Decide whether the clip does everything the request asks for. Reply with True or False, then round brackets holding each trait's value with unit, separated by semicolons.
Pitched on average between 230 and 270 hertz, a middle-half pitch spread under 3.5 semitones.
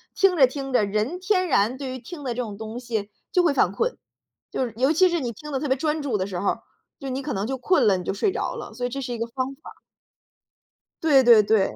False (260 Hz; 5.2 semitones)